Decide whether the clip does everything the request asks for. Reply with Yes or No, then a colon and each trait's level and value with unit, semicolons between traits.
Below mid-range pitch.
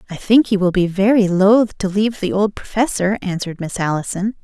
No: high, 195 Hz